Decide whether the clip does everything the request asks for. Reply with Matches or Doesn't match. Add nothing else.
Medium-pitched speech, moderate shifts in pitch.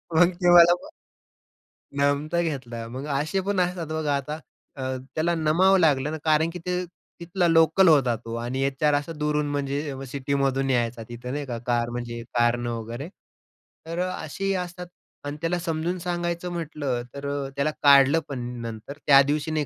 Matches